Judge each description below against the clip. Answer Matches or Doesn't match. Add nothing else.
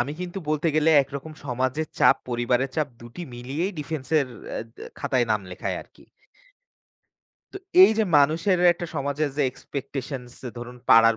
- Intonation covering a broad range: Doesn't match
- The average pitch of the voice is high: Doesn't match